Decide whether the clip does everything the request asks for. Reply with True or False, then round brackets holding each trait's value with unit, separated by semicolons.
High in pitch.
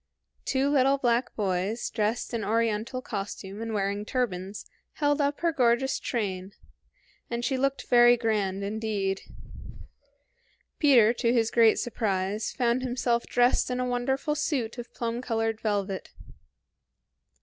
True (235 Hz)